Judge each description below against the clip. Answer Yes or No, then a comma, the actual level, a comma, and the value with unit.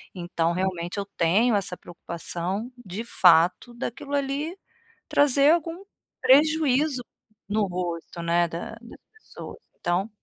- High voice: Yes, high, 205 Hz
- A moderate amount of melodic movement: No, wide, 7.5 semitones